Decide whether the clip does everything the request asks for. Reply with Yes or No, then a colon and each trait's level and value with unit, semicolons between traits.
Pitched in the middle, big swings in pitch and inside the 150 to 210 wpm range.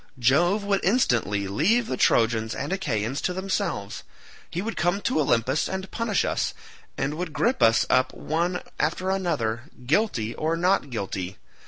Yes: medium, 155 Hz; wide, 8.5 semitones; average, 155 wpm